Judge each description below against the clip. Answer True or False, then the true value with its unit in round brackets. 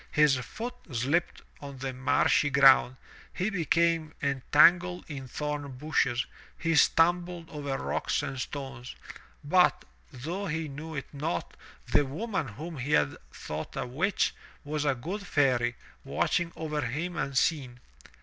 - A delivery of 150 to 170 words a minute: False (135 wpm)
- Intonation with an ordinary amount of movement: True (3.9 semitones)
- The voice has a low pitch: False (150 Hz)